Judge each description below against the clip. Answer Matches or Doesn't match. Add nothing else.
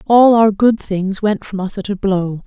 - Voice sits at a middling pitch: Doesn't match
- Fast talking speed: Matches